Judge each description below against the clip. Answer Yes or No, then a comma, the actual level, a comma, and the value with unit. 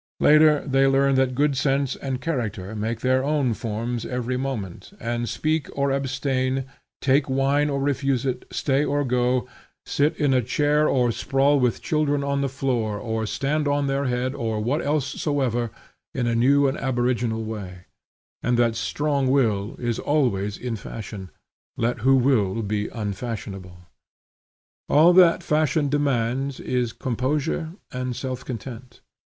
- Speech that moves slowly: No, average, 150 wpm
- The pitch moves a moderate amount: Yes, average, 3.2 semitones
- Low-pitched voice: Yes, low, 130 Hz